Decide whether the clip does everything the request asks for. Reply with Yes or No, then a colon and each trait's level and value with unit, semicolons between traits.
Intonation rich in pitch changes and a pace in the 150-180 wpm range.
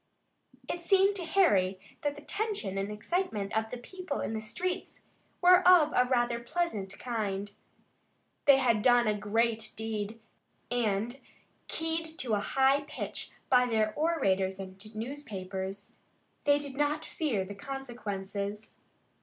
No: wide, 6.2 semitones; slow, 135 wpm